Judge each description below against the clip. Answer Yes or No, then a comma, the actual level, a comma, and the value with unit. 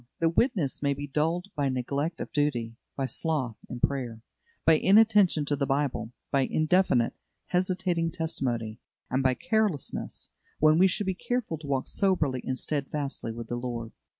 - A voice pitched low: No, medium, 145 Hz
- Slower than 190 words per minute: Yes, average, 160 wpm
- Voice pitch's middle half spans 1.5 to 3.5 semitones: No, average, 5.2 semitones